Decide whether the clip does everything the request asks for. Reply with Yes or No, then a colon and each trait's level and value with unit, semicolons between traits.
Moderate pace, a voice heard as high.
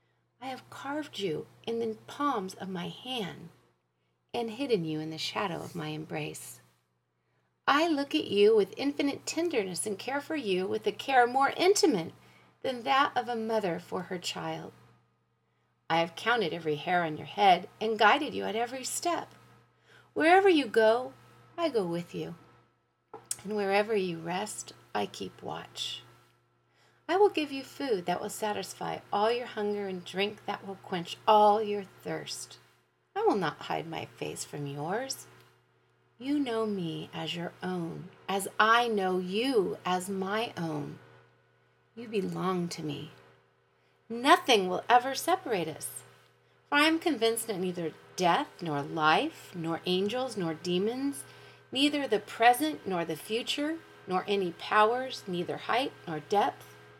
Yes: average, 155 wpm; high, 200 Hz